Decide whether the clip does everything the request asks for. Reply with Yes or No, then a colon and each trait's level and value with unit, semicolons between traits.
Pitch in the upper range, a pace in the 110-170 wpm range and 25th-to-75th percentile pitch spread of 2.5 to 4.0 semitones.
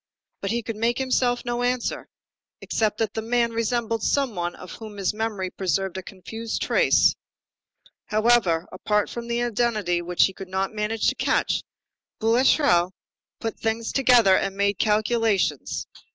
Yes: high, 220 Hz; average, 150 wpm; average, 3.5 semitones